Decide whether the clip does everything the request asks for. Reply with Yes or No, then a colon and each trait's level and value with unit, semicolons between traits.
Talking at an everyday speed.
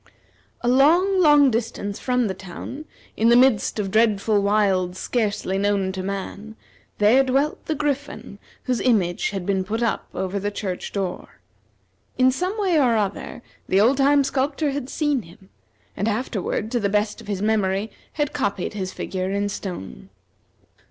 Yes: average, 165 wpm